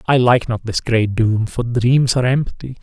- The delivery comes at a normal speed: No, fast, 210 wpm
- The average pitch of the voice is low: Yes, low, 120 Hz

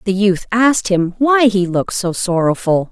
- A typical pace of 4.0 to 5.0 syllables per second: Yes, 4.8 syllables/s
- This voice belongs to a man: No, female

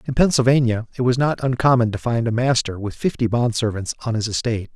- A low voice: Yes, low, 120 Hz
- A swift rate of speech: Yes, fast, 215 wpm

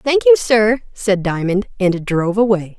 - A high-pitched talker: Yes, high, 205 Hz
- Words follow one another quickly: No, average, 170 wpm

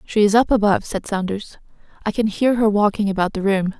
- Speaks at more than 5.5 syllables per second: Yes, 5.9 syllables/s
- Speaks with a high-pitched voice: Yes, high, 205 Hz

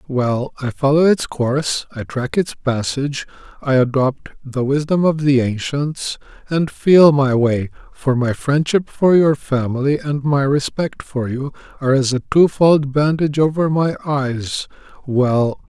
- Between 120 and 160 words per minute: Yes, average, 150 wpm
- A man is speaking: Yes, male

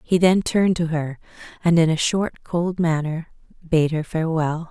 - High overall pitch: No, medium, 165 Hz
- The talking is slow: No, average, 180 wpm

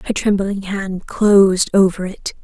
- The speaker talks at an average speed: Yes, average, 150 wpm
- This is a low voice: No, high, 195 Hz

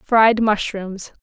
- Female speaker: Yes, female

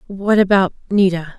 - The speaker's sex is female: Yes, female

